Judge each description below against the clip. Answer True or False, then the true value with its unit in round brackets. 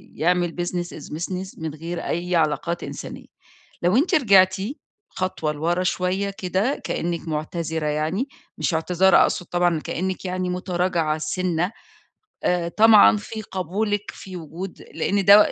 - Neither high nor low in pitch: True (180 Hz)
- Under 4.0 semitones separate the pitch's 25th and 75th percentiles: True (2.4 semitones)